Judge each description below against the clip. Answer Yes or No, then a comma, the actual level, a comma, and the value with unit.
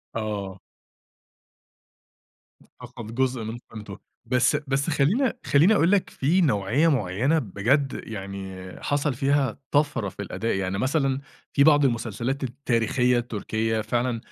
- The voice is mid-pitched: No, low, 125 Hz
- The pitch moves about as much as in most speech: Yes, average, 4.7 semitones